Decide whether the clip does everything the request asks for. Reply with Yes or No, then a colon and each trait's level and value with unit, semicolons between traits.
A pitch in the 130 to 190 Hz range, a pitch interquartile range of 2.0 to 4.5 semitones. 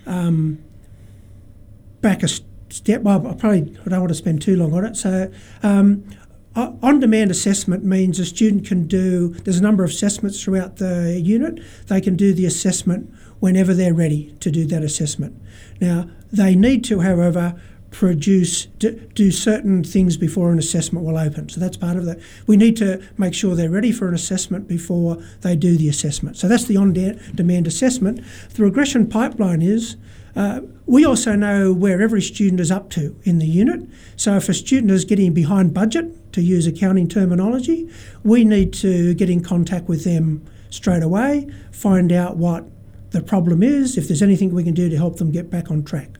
Yes: medium, 185 Hz; average, 3.1 semitones